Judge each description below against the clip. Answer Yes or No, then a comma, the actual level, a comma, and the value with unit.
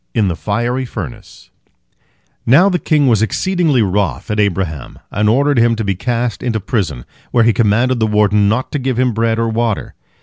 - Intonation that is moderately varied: Yes, average, 3.4 semitones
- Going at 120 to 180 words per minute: No, average, 190 wpm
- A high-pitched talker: No, low, 115 Hz